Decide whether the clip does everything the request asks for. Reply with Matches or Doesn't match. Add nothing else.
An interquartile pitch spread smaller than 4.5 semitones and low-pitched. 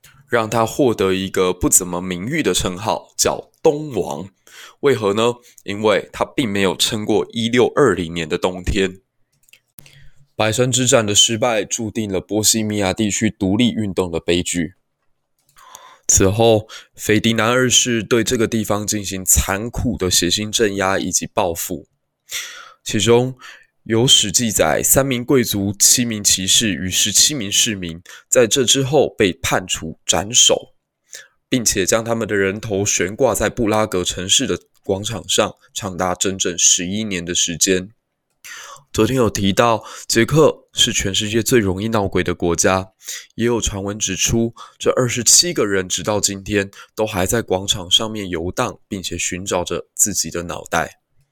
Matches